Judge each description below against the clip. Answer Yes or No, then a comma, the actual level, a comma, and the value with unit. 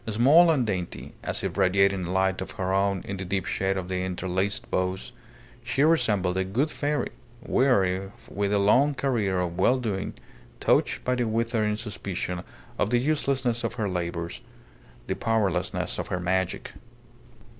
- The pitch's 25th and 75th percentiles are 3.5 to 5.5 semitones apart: Yes, average, 4.4 semitones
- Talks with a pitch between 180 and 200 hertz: No, low, 100 Hz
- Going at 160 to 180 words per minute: Yes, average, 165 wpm